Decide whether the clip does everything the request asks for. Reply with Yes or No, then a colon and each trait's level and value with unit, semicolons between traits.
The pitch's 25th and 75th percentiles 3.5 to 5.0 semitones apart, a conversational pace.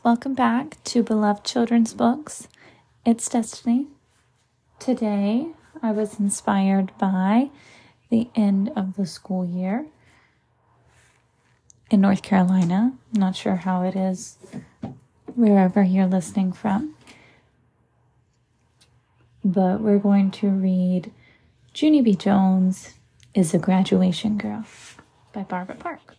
No: average, 3.8 semitones; slow, 110 wpm